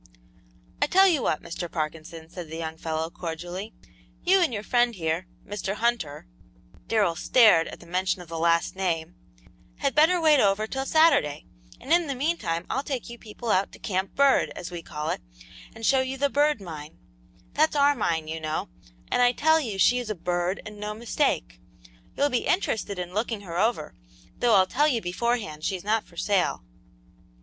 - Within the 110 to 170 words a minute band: No, average, 195 wpm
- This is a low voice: No, high, 205 Hz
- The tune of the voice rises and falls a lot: Yes, wide, 7.2 semitones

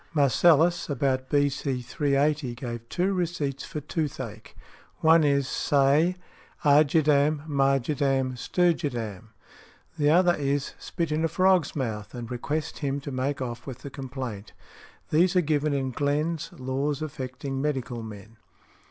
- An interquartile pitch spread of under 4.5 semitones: Yes, average, 3.0 semitones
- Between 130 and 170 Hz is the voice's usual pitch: Yes, medium, 140 Hz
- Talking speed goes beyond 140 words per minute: No, slow, 135 wpm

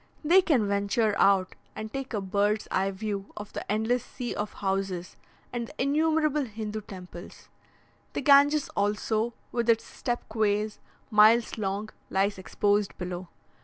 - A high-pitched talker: Yes, high, 215 Hz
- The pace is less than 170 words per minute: Yes, average, 145 wpm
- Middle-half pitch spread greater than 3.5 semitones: No, average, 3.2 semitones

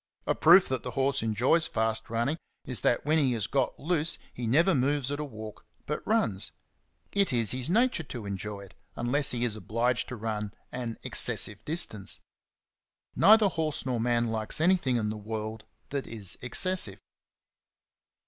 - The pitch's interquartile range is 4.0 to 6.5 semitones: Yes, average, 5.3 semitones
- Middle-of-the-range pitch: No, low, 125 Hz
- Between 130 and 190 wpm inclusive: Yes, average, 165 wpm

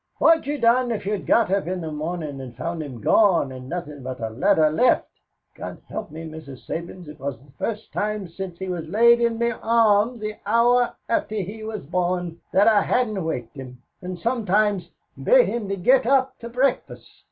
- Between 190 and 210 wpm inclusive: Yes, average, 200 wpm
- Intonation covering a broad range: Yes, wide, 6.5 semitones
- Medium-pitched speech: No, high, 195 Hz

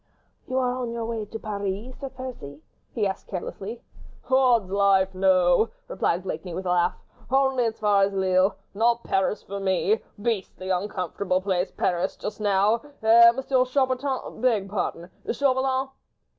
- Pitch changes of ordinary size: Yes, average, 4.5 semitones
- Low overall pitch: No, high, 205 Hz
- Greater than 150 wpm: No, average, 145 wpm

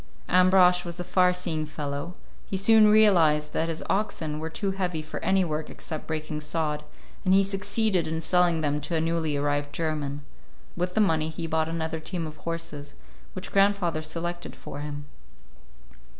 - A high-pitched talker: No, medium, 165 Hz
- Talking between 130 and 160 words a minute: No, average, 170 wpm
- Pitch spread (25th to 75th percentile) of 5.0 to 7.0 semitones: No, average, 2.9 semitones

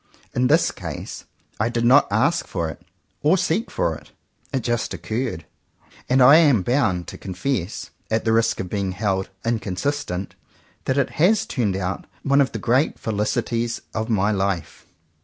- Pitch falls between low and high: No, low, 115 Hz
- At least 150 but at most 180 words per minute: Yes, average, 170 wpm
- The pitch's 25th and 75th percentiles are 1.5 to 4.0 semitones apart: No, wide, 5.4 semitones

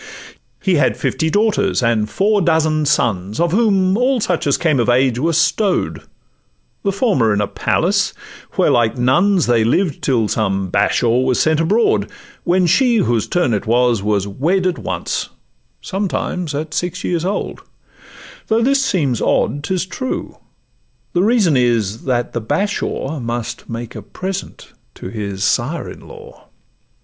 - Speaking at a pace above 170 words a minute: No, average, 155 wpm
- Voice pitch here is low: No, medium, 155 Hz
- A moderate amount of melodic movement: No, wide, 8.1 semitones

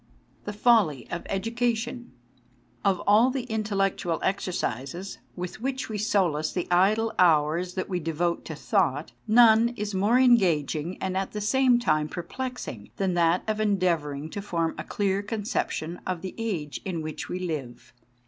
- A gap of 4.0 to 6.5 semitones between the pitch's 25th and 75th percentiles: Yes, average, 4.8 semitones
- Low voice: No, high, 190 Hz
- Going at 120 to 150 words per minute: No, average, 160 wpm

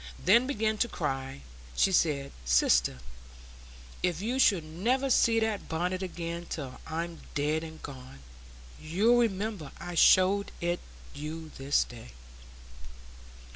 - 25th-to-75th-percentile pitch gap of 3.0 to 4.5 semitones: No, average, 5.3 semitones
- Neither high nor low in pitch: Yes, medium, 170 Hz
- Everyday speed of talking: No, slow, 125 wpm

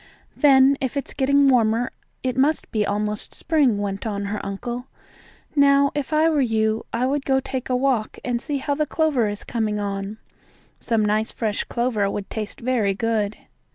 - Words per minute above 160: Yes, average, 180 wpm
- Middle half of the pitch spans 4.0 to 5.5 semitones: Yes, average, 4.4 semitones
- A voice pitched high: Yes, high, 240 Hz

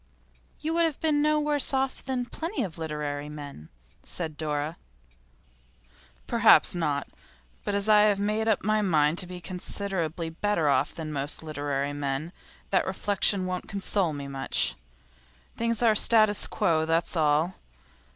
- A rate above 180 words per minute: No, average, 150 wpm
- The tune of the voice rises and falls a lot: Yes, wide, 6.0 semitones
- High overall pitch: No, medium, 175 Hz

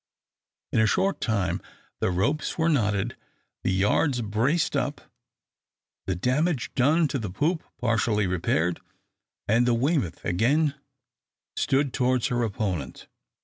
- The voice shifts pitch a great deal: Yes, wide, 6.3 semitones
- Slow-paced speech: Yes, slow, 125 wpm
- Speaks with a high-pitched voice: No, low, 120 Hz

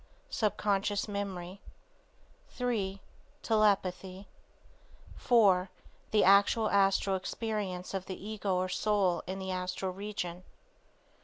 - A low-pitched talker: No, high, 195 Hz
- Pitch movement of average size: No, narrow, 2.1 semitones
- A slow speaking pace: Yes, slow, 95 wpm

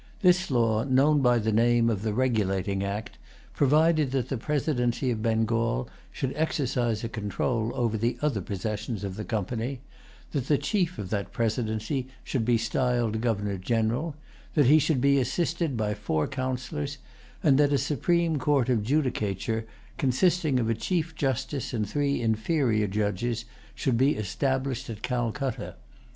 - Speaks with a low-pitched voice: Yes, low, 120 Hz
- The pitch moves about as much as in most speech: Yes, average, 4.2 semitones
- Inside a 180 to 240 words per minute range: No, average, 155 wpm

